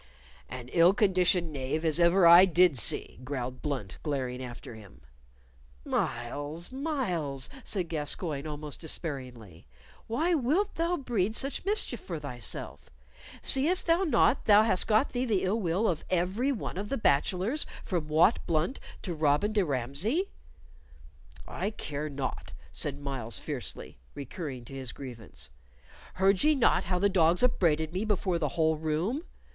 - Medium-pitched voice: Yes, medium, 170 Hz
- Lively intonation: Yes, wide, 7.2 semitones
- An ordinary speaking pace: Yes, average, 150 wpm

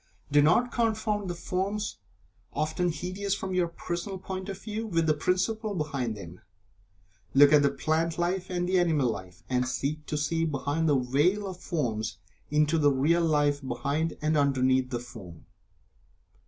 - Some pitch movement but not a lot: Yes, average, 4.6 semitones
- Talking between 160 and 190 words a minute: Yes, average, 165 wpm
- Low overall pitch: No, medium, 160 Hz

